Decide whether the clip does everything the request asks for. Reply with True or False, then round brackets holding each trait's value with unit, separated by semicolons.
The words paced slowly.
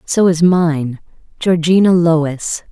True (110 wpm)